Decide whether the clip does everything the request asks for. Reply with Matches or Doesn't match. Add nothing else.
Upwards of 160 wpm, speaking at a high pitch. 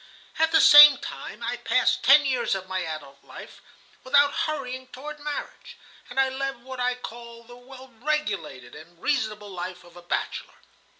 Matches